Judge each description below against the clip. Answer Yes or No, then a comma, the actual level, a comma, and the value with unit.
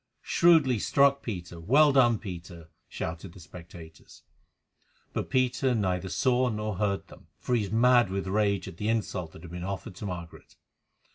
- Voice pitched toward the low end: Yes, low, 100 Hz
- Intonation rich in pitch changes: Yes, wide, 5.7 semitones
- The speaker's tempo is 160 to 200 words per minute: Yes, average, 165 wpm